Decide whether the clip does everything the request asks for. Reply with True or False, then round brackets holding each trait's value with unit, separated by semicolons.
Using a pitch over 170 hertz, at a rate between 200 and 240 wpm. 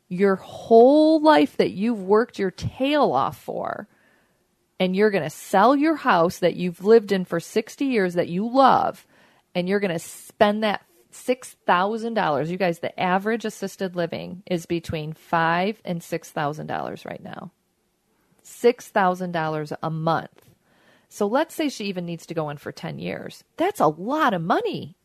False (190 Hz; 175 wpm)